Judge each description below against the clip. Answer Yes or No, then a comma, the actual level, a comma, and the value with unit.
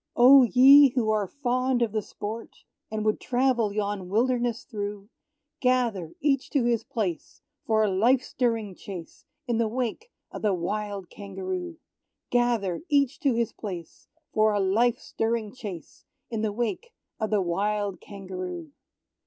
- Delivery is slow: No, average, 150 wpm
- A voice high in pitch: Yes, high, 220 Hz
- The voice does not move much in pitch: No, average, 3.7 semitones